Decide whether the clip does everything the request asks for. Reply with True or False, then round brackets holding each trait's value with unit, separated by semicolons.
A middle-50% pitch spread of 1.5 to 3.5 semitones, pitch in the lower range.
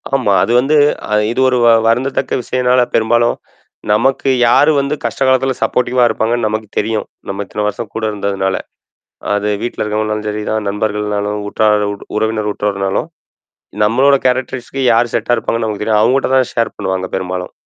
True (3.2 semitones; 110 Hz)